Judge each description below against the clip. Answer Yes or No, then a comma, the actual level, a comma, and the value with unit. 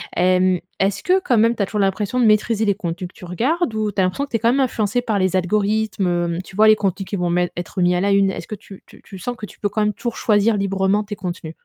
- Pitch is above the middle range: Yes, high, 200 Hz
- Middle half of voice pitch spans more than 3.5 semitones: No, average, 2.9 semitones